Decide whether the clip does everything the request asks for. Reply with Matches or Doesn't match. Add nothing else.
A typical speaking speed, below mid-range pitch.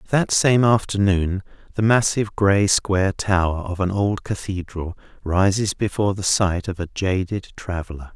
Matches